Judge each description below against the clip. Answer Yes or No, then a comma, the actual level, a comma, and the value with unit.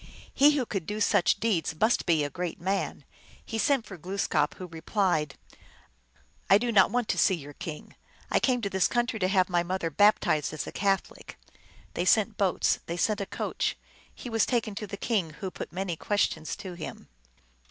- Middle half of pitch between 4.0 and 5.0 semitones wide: Yes, average, 4.4 semitones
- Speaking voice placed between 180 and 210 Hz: Yes, high, 190 Hz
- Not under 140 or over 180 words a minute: No, average, 195 wpm